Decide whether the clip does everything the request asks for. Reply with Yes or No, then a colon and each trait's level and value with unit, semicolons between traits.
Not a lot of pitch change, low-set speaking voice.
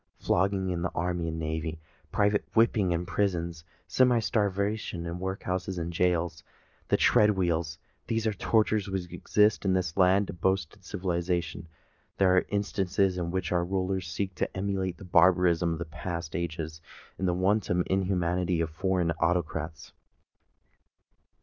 Yes: narrow, 2.3 semitones; very low, 90 Hz